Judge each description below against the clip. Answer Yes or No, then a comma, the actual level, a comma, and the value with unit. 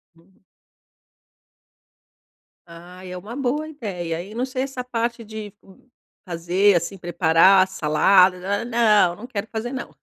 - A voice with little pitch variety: No, average, 5.0 semitones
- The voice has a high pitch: Yes, high, 195 Hz